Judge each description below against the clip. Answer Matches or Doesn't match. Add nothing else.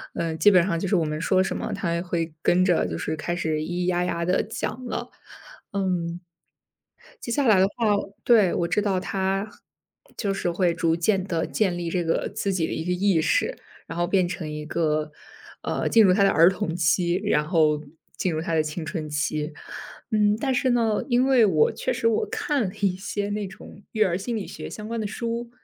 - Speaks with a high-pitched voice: Doesn't match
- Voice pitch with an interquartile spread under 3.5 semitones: Doesn't match